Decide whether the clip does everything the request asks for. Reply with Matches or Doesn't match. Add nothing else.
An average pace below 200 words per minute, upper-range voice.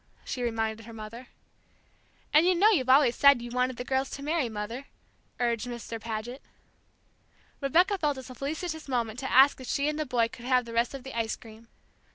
Doesn't match